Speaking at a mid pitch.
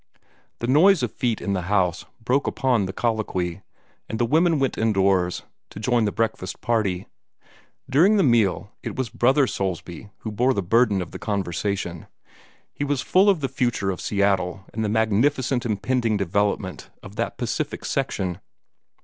No: low, 110 Hz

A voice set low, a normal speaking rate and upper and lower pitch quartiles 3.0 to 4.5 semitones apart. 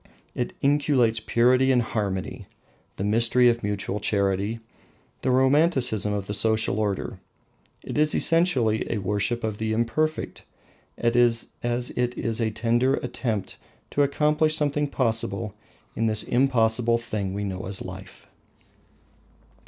No: low, 115 Hz; slow, 130 wpm; average, 3.6 semitones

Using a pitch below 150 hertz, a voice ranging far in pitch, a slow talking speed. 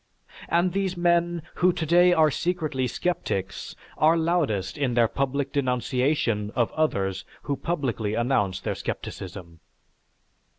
Yes: medium, 140 Hz; wide, 6.6 semitones; slow, 120 wpm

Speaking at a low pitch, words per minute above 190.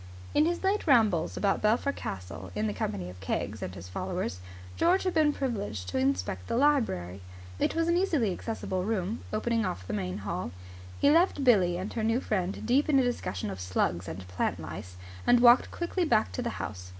No: high, 200 Hz; average, 200 wpm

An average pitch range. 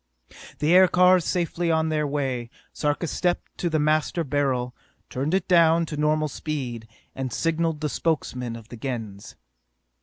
Yes: average, 4.2 semitones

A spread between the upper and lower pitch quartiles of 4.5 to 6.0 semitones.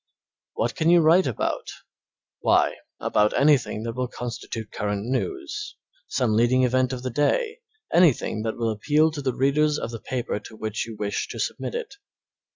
Yes: average, 5.2 semitones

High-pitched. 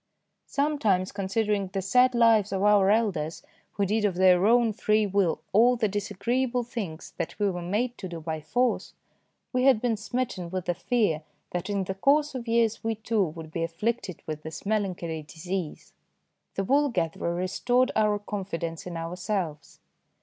Yes: high, 200 Hz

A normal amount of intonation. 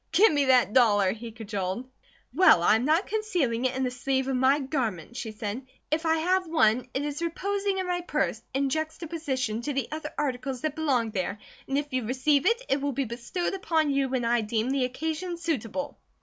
Yes: average, 4.9 semitones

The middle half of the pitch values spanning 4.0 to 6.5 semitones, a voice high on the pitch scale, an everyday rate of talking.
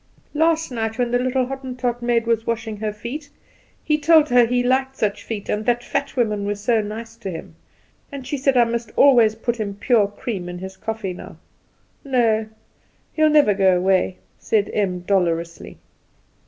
No: average, 3.6 semitones; high, 230 Hz; average, 175 wpm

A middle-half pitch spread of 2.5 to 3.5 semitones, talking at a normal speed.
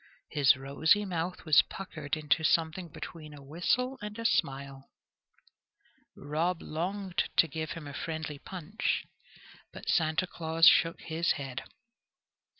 No: average, 3.1 semitones; slow, 130 wpm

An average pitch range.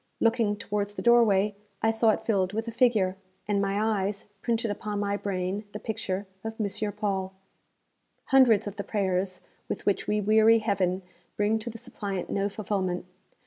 No: narrow, 2.1 semitones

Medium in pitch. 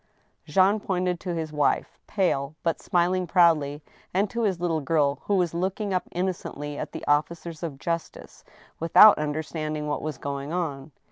Yes: medium, 165 Hz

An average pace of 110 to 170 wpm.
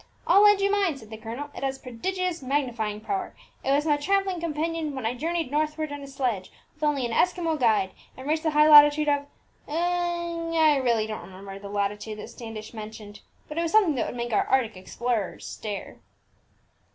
No: average, 195 wpm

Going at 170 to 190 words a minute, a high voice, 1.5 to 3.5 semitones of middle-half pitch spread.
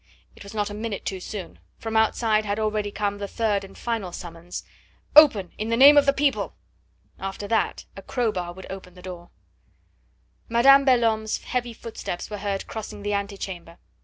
Yes: average, 185 wpm; high, 210 Hz; average, 2.9 semitones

